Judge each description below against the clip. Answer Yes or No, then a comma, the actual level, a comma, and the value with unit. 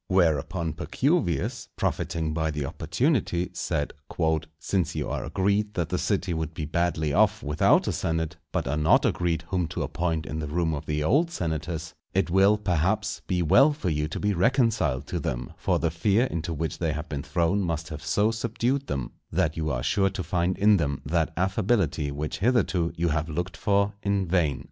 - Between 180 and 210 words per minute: Yes, average, 190 wpm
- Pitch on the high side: No, very low, 85 Hz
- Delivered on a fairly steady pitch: No, average, 4.1 semitones